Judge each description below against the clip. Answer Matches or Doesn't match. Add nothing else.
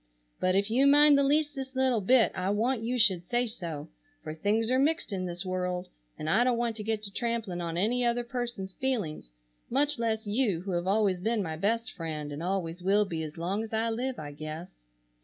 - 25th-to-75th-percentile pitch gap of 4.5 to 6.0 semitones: Matches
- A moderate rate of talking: Doesn't match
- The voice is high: Matches